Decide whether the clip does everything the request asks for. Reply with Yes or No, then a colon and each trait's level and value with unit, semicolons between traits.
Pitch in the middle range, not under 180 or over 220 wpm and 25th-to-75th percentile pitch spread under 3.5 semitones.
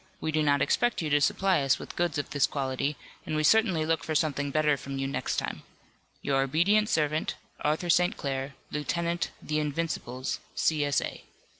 Yes: medium, 150 Hz; average, 185 wpm; average, 2.8 semitones